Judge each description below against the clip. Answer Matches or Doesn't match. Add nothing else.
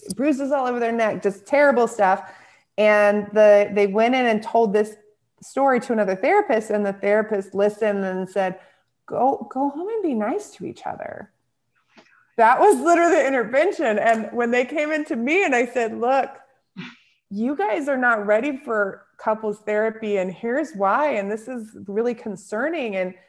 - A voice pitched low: Doesn't match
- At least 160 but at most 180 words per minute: Matches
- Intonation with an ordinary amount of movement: Matches